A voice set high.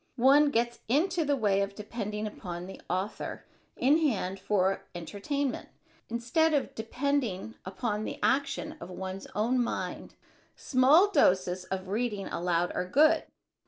Yes: high, 220 Hz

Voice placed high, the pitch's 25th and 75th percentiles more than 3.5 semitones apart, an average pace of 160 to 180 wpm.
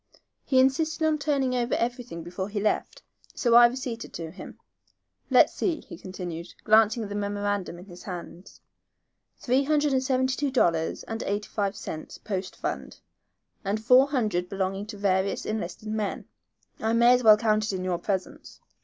Yes: high, 215 Hz; average, 4.8 semitones; average, 170 wpm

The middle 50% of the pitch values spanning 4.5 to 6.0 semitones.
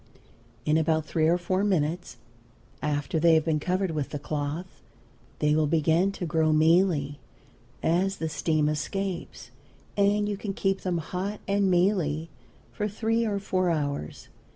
No: average, 4.0 semitones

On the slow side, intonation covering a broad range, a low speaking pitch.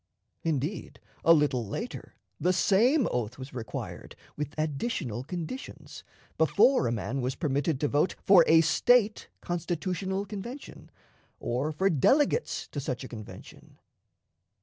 No: slow, 125 wpm; wide, 6.7 semitones; medium, 160 Hz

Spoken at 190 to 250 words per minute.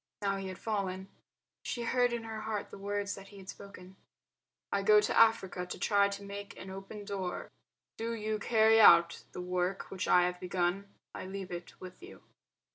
Yes: average, 195 wpm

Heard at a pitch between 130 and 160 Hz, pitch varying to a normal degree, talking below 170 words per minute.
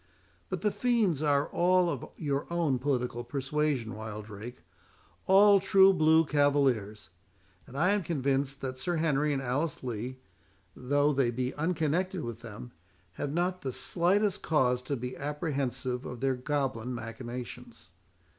Yes: medium, 140 Hz; average, 4.6 semitones; average, 140 wpm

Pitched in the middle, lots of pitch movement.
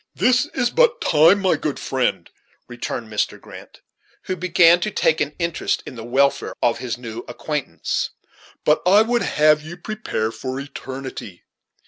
Yes: medium, 150 Hz; wide, 6.2 semitones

